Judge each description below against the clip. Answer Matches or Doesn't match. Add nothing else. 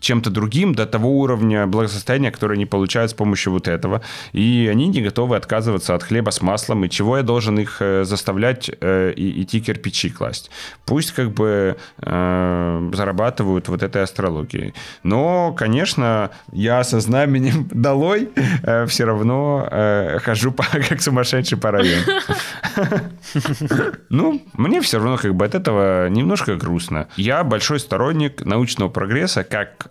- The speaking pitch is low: Matches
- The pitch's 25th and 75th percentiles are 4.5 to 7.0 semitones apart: Matches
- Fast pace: Doesn't match